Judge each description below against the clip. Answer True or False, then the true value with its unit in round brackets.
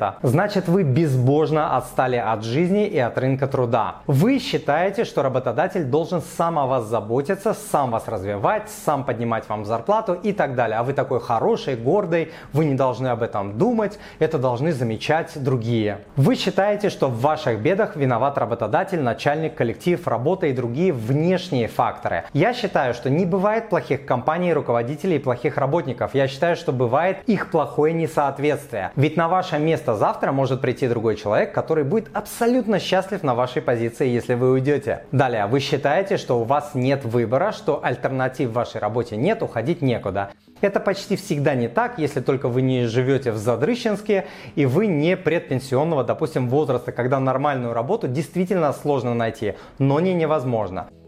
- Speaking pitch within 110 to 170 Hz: True (140 Hz)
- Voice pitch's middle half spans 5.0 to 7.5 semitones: True (5.5 semitones)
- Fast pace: True (165 wpm)